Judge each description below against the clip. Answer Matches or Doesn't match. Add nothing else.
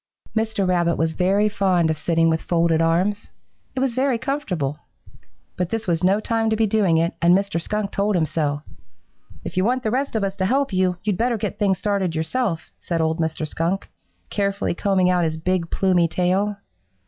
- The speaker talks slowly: Doesn't match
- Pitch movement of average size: Matches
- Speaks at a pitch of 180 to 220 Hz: Matches